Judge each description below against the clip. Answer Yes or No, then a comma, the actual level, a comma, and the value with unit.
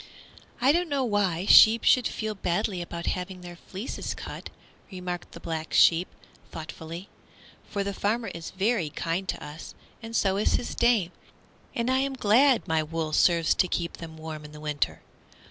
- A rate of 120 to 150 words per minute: No, average, 175 wpm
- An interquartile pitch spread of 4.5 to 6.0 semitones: Yes, average, 5.2 semitones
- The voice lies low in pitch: No, medium, 185 Hz